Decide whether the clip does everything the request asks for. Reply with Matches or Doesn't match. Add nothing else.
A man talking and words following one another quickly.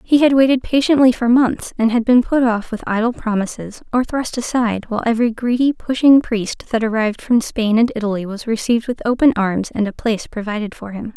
Doesn't match